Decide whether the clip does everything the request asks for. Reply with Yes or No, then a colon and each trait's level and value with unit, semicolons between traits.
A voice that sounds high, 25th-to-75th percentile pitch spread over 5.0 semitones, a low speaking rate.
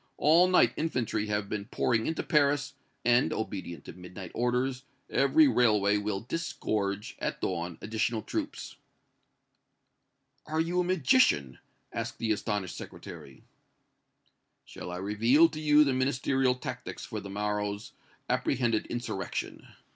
No: low, 115 Hz; wide, 5.6 semitones; slow, 125 wpm